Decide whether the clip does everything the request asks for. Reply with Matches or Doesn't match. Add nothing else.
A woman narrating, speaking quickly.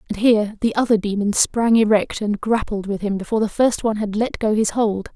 Matches